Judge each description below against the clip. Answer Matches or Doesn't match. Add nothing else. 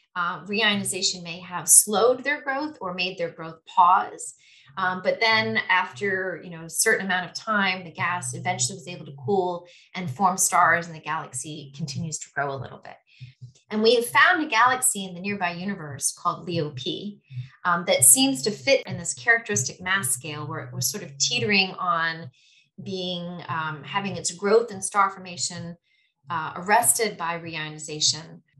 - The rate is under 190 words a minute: Matches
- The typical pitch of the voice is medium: Matches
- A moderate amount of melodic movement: Matches